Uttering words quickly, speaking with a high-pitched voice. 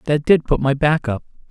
No: fast, 240 wpm; medium, 145 Hz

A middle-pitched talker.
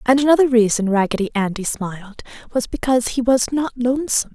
No: high, 240 Hz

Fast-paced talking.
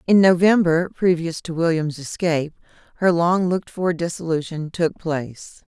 No: slow, 135 wpm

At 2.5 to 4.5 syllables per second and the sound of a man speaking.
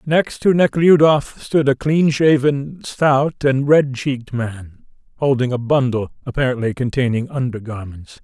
Yes: 4.3 syllables/s; male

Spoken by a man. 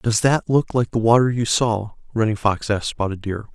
Yes: male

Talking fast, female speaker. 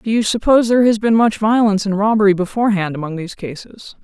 Yes: fast, 210 wpm; female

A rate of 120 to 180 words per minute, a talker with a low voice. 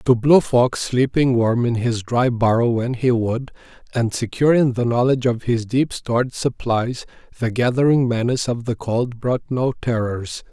Yes: average, 175 wpm; low, 120 Hz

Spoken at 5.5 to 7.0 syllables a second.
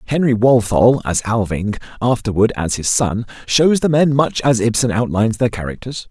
No: 5.0 syllables/s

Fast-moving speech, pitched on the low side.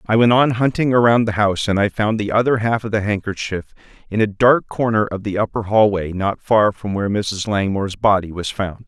Yes: fast, 225 wpm; low, 105 Hz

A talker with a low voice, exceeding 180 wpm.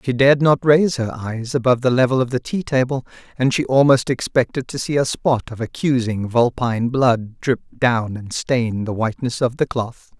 Yes: low, 125 Hz; average, 200 wpm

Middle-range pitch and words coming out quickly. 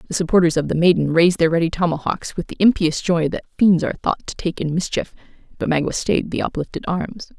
Yes: medium, 170 Hz; fast, 220 wpm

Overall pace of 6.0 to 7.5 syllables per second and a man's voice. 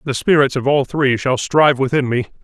No: 5.6 syllables/s; male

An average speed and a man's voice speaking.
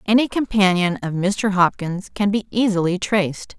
No: average, 150 wpm; female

